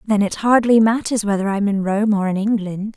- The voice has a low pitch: No, high, 210 Hz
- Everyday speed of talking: No, fast, 225 wpm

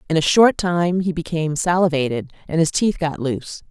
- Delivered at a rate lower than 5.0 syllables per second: No, 5.5 syllables/s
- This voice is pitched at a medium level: Yes, medium, 165 Hz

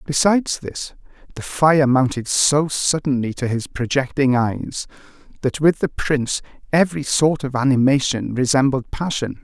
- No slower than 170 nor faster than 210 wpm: No, slow, 135 wpm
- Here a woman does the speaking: No, male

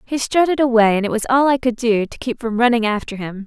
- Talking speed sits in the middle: No, fast, 275 wpm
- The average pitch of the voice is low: No, high, 235 Hz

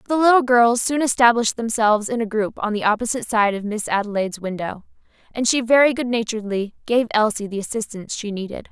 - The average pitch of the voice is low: No, high, 225 Hz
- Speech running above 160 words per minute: Yes, average, 195 wpm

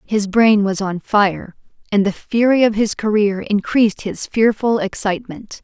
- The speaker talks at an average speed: Yes, average, 160 wpm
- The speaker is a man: No, female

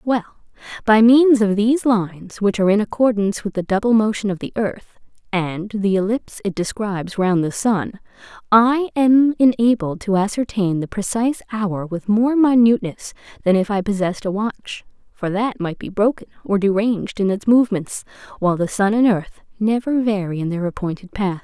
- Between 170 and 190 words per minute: Yes, average, 175 wpm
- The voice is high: Yes, high, 210 Hz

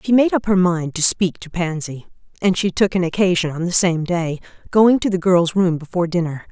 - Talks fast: Yes, fast, 230 wpm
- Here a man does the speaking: No, female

